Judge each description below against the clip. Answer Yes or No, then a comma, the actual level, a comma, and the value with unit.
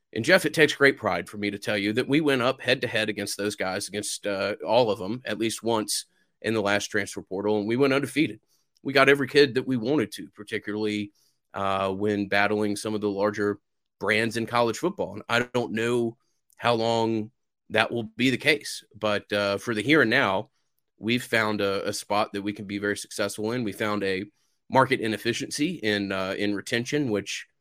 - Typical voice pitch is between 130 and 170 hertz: No, low, 110 Hz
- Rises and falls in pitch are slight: No, average, 3.3 semitones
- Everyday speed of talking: No, fast, 215 wpm